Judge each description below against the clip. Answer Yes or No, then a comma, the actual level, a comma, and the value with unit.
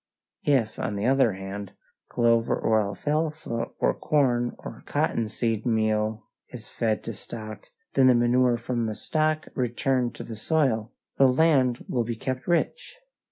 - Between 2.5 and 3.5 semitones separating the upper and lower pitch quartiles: Yes, average, 3.2 semitones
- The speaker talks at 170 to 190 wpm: No, average, 155 wpm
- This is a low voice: Yes, low, 120 Hz